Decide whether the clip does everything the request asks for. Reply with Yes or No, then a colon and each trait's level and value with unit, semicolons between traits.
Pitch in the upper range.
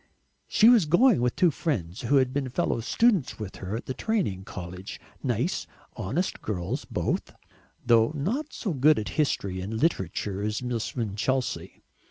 No: low, 125 Hz